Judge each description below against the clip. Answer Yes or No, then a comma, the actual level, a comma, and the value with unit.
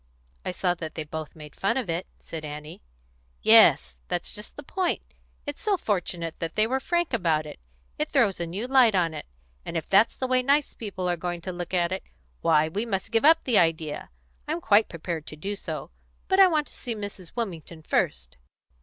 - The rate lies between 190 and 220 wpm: Yes, fast, 205 wpm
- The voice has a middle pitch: Yes, medium, 180 Hz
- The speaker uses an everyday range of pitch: No, wide, 6.1 semitones